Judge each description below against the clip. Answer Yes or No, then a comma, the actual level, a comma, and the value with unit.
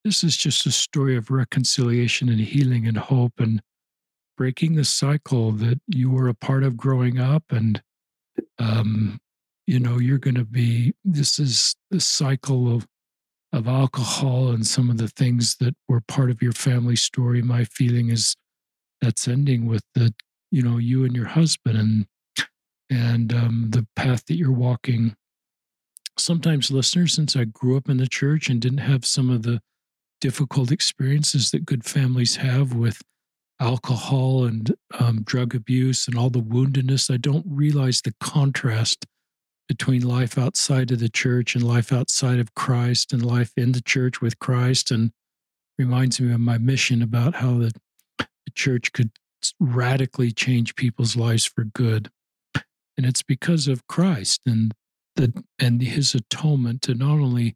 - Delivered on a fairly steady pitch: Yes, narrow, 2.2 semitones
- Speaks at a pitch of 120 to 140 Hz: Yes, low, 125 Hz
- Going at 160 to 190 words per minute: Yes, average, 165 wpm